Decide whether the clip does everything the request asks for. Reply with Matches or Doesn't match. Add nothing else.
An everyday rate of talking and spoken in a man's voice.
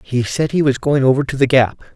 Doesn't match